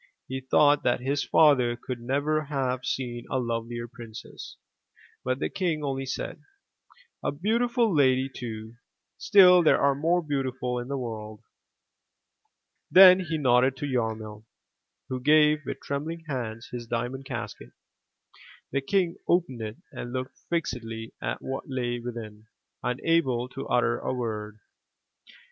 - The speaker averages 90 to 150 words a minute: Yes, slow, 135 wpm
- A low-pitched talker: Yes, low, 130 Hz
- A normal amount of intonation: Yes, average, 3.9 semitones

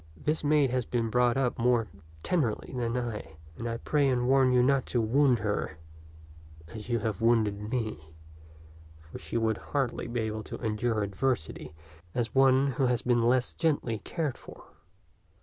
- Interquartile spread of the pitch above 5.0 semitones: No, average, 2.9 semitones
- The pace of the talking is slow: No, average, 165 wpm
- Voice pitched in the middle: No, low, 120 Hz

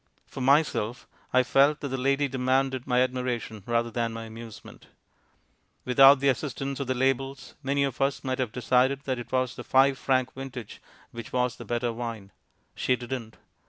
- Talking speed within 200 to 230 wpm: No, average, 175 wpm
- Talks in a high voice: No, low, 130 Hz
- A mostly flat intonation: Yes, narrow, 2.1 semitones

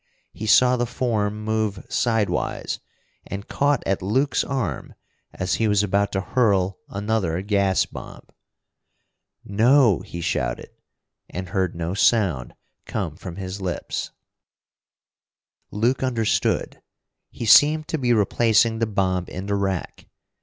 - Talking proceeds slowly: Yes, slow, 125 wpm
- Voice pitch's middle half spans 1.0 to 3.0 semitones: No, average, 3.6 semitones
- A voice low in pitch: Yes, low, 105 Hz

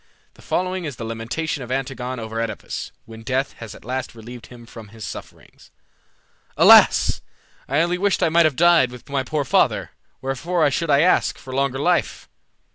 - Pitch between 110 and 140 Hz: Yes, low, 135 Hz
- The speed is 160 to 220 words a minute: Yes, average, 180 wpm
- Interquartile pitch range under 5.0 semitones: No, wide, 5.4 semitones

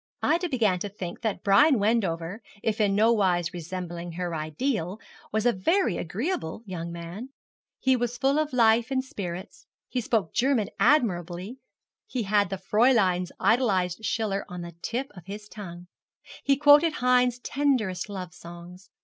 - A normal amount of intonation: No, wide, 5.7 semitones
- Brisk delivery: No, average, 150 wpm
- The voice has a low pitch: No, high, 210 Hz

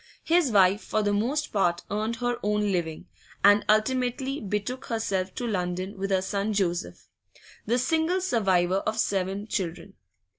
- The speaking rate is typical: Yes, average, 150 wpm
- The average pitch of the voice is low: No, high, 210 Hz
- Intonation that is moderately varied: Yes, average, 4.1 semitones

